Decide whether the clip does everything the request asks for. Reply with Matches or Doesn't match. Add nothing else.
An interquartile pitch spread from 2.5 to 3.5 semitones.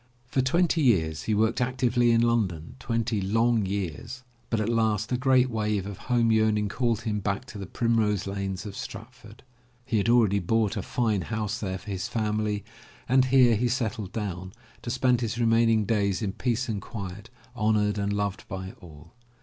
Matches